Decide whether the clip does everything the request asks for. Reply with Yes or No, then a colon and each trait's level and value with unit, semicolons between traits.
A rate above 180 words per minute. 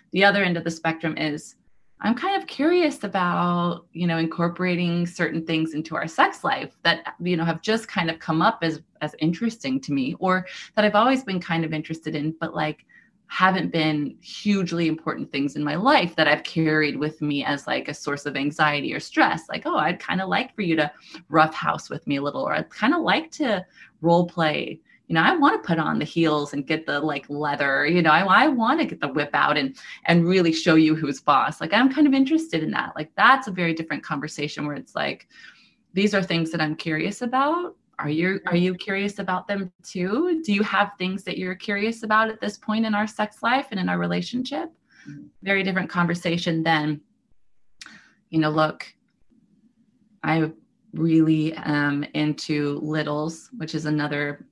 Yes: fast, 205 wpm